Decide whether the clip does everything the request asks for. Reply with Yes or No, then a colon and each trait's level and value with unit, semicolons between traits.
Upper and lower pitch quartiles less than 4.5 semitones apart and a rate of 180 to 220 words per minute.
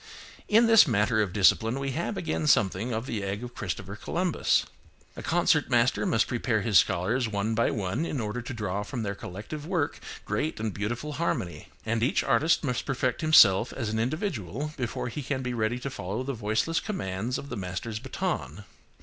No: average, 5.2 semitones; average, 190 wpm